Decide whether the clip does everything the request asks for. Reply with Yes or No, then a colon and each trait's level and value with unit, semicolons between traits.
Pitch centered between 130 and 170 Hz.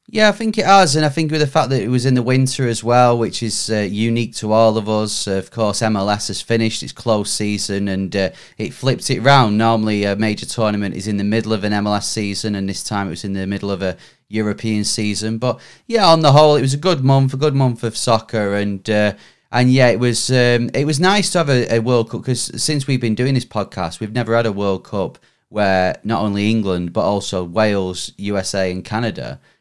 No: low, 110 Hz